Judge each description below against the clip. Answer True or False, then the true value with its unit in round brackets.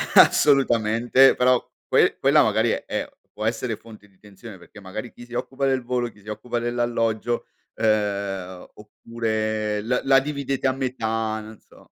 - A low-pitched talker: True (115 Hz)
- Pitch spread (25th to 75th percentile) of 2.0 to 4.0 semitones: True (2.7 semitones)